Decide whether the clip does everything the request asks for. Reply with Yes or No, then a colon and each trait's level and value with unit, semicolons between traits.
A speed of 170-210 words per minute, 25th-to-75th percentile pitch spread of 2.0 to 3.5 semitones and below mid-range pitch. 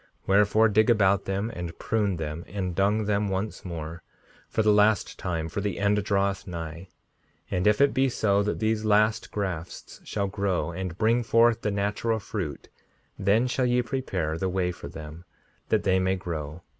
Yes: average, 180 wpm; average, 3.2 semitones; low, 100 Hz